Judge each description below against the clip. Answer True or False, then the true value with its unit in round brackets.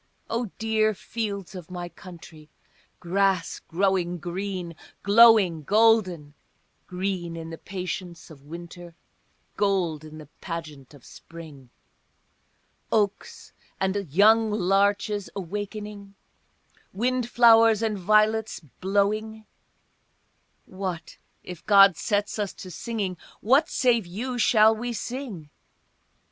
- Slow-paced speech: True (105 wpm)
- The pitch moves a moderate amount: True (3.9 semitones)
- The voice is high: True (195 Hz)